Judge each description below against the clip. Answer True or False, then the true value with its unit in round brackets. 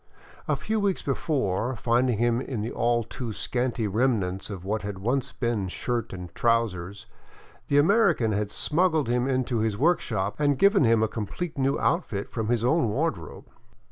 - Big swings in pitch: False (4.6 semitones)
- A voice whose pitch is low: True (120 Hz)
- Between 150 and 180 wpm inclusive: True (170 wpm)